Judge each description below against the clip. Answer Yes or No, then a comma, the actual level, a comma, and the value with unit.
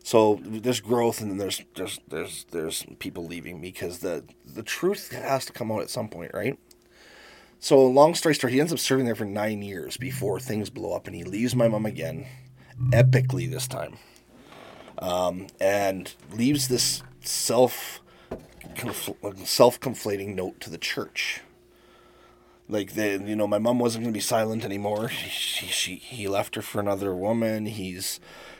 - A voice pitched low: Yes, low, 115 Hz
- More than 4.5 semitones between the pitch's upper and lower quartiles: No, average, 4.1 semitones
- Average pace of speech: Yes, average, 170 wpm